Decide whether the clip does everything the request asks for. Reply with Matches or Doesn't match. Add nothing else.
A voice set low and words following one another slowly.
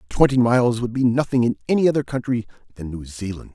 Doesn't match